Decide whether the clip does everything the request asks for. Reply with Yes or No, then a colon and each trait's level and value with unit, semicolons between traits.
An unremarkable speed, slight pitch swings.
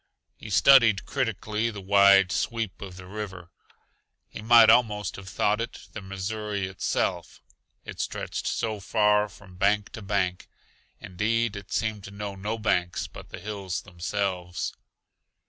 Yes: average, 145 wpm; narrow, 2.2 semitones